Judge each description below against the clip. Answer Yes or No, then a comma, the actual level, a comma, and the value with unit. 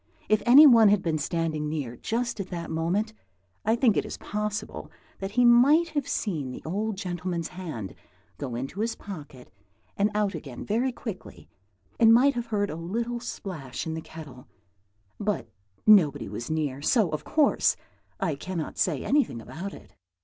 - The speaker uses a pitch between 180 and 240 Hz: Yes, high, 190 Hz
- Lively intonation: Yes, wide, 6.3 semitones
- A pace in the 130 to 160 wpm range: No, average, 170 wpm